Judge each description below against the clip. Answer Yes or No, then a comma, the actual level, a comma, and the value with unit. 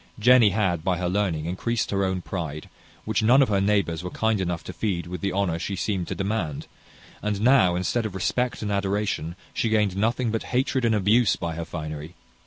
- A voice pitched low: Yes, low, 100 Hz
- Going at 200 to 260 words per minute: Yes, fast, 205 wpm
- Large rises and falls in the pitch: No, average, 3.8 semitones